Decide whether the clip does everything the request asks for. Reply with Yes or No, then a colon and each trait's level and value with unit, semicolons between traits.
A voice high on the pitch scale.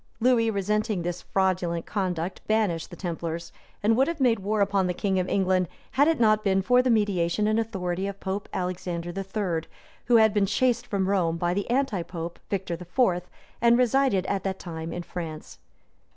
Yes: high, 195 Hz